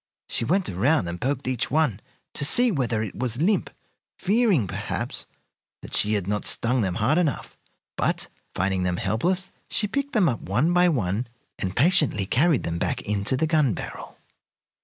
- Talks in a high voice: No, low, 130 Hz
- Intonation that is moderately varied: No, wide, 8.8 semitones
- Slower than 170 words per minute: No, average, 175 wpm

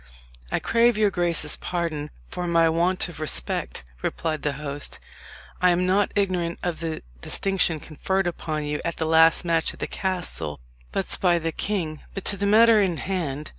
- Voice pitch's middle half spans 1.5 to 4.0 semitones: Yes, average, 3.3 semitones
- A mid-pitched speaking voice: Yes, medium, 170 Hz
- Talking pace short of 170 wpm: No, average, 175 wpm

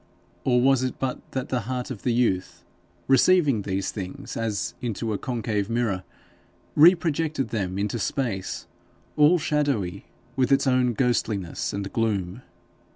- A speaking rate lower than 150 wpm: Yes, average, 140 wpm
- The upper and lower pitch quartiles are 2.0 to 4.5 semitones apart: No, average, 4.9 semitones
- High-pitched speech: No, low, 120 Hz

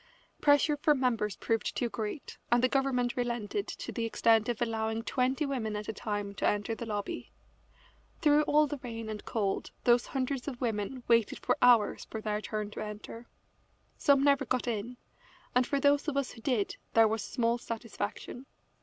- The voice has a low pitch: No, high, 235 Hz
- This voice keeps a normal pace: Yes, average, 180 wpm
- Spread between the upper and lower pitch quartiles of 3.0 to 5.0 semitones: Yes, average, 3.5 semitones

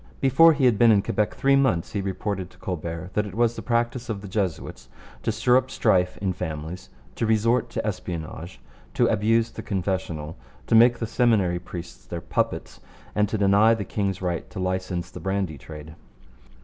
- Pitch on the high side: No, low, 100 Hz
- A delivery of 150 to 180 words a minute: No, average, 190 wpm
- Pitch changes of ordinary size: Yes, average, 4.1 semitones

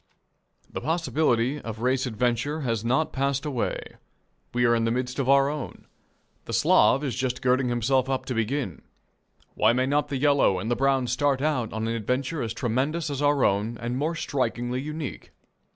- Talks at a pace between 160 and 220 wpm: Yes, average, 185 wpm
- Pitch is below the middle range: Yes, low, 130 Hz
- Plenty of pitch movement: No, average, 3.2 semitones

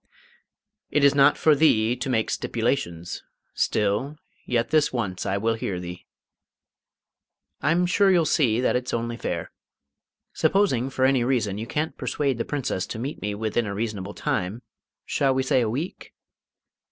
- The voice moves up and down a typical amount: Yes, average, 4.5 semitones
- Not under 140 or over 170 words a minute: Yes, average, 160 wpm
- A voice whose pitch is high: No, low, 120 Hz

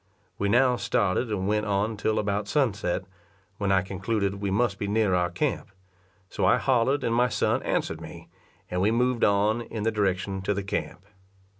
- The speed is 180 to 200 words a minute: Yes, average, 185 wpm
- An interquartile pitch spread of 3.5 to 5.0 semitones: No, average, 2.8 semitones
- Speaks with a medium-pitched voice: No, low, 105 Hz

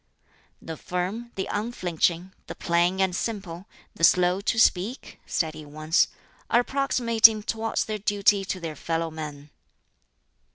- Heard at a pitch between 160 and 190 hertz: Yes, medium, 185 Hz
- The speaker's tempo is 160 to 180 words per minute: No, slow, 135 wpm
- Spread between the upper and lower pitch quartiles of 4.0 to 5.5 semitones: Yes, average, 4.6 semitones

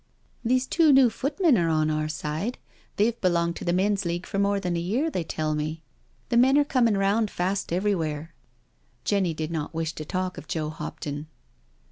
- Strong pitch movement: Yes, wide, 5.9 semitones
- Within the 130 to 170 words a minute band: No, fast, 205 wpm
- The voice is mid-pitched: Yes, medium, 180 Hz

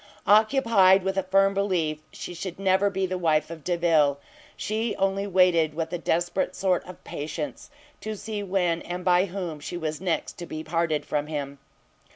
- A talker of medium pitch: Yes, medium, 180 Hz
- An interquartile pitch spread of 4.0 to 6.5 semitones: No, average, 3.2 semitones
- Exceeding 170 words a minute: Yes, average, 180 wpm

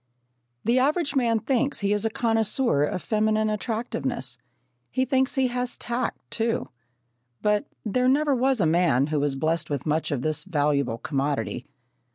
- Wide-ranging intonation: Yes, wide, 8.4 semitones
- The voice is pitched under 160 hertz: No, high, 215 Hz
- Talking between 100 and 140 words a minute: No, average, 160 wpm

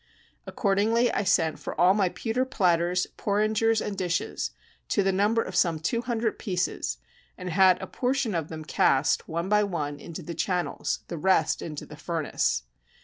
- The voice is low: No, medium, 185 Hz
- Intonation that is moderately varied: Yes, average, 4.2 semitones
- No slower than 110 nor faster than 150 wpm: No, average, 170 wpm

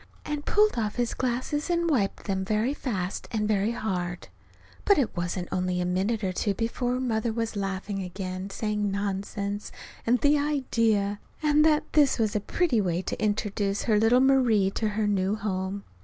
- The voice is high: Yes, high, 210 Hz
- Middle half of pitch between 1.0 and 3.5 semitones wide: No, average, 4.1 semitones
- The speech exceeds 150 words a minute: Yes, average, 180 wpm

